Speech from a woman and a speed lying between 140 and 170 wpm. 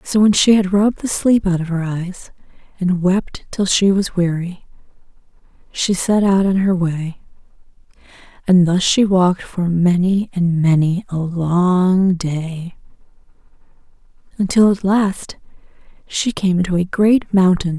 Yes: female; average, 145 wpm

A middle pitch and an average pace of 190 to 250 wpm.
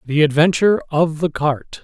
No: medium, 160 Hz; average, 165 wpm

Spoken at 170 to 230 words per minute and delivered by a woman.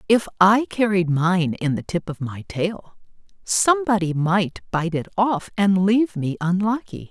No: average, 160 wpm; female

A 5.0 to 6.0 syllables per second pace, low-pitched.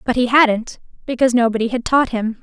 No: 5.9 syllables/s; high, 240 Hz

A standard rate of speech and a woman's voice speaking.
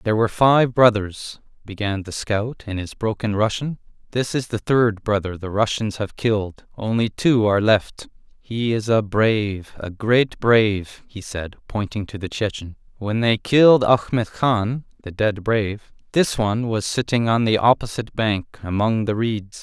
No: average, 170 wpm; male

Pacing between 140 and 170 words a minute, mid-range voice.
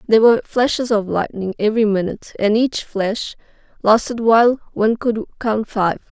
No: average, 155 wpm; high, 220 Hz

